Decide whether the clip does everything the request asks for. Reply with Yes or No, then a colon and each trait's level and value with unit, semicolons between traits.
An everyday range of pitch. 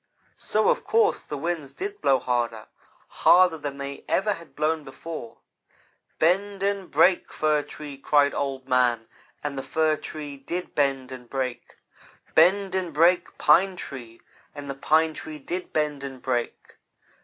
Yes: average, 4.5 semitones